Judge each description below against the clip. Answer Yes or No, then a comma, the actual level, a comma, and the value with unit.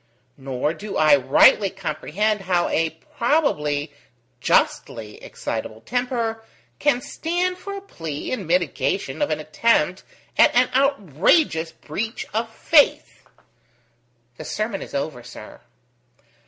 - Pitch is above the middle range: Yes, high, 195 Hz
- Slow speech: Yes, slow, 115 wpm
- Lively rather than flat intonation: Yes, wide, 8.3 semitones